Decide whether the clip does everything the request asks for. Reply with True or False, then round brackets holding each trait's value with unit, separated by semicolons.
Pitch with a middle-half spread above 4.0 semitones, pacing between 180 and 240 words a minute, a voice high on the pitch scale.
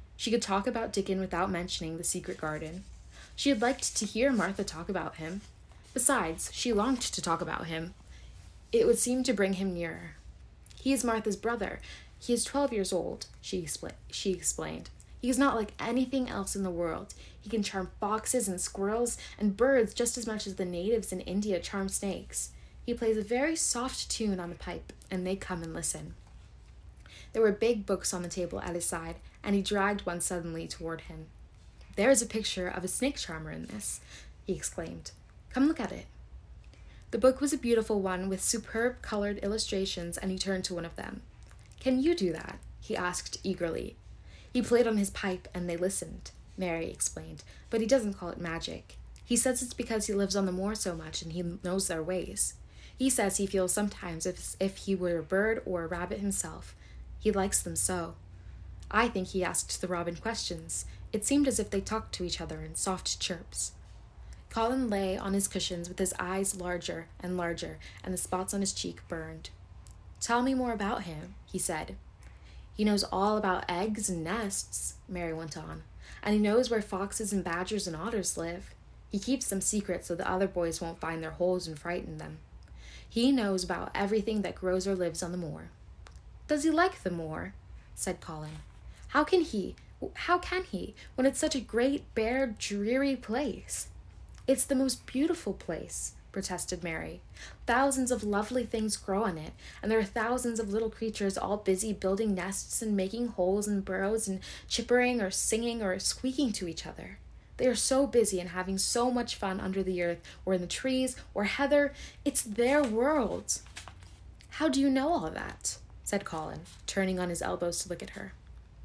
True (4.8 semitones; 190 wpm; 195 Hz)